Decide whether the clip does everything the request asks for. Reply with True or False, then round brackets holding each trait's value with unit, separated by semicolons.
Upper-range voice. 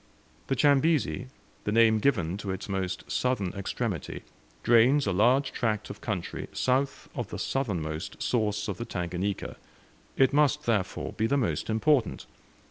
False (110 Hz)